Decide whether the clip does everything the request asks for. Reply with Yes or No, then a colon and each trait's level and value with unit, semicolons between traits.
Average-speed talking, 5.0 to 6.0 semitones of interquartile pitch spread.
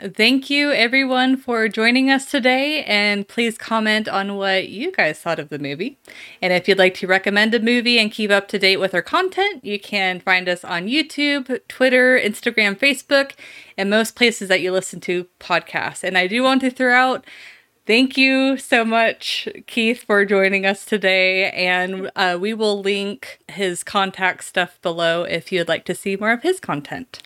Yes: average, 185 wpm; average, 5.3 semitones